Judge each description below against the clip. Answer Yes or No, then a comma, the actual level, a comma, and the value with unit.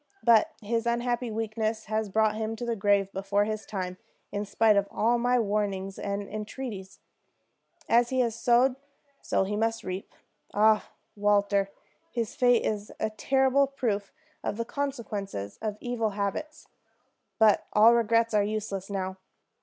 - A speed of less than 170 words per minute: Yes, average, 150 wpm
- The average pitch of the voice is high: Yes, high, 215 Hz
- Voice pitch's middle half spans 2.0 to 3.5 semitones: Yes, average, 2.7 semitones